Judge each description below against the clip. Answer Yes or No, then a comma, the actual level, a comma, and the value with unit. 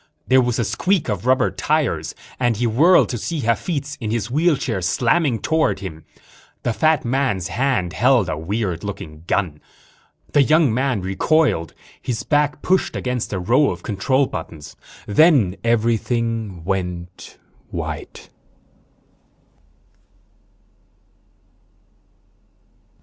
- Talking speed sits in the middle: No, slow, 115 wpm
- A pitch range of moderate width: No, wide, 6.6 semitones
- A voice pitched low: Yes, low, 115 Hz